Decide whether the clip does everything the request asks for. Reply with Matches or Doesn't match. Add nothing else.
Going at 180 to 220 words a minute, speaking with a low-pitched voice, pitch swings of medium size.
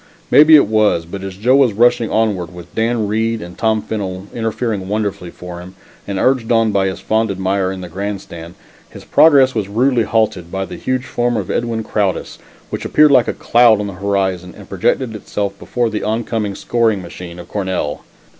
Matches